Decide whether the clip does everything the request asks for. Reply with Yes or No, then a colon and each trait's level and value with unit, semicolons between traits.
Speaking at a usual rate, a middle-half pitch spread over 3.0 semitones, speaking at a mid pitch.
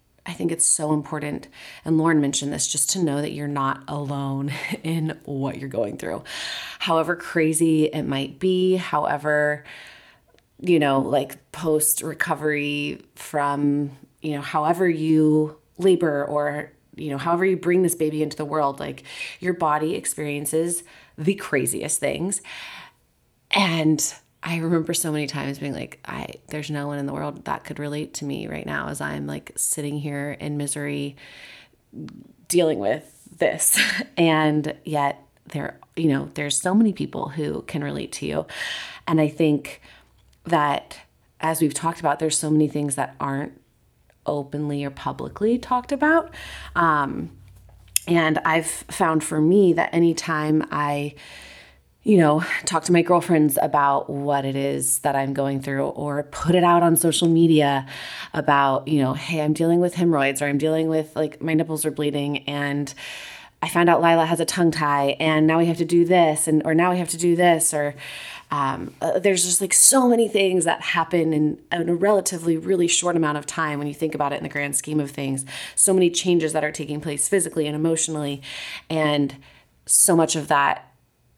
No: average, 175 wpm; average, 2.7 semitones; medium, 155 Hz